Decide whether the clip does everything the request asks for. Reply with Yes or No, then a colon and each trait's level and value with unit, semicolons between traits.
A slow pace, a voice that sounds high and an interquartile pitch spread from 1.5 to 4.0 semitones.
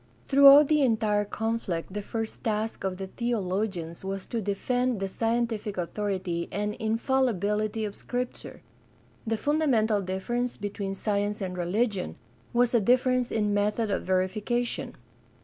Yes: slow, 130 wpm; high, 215 Hz; average, 3.5 semitones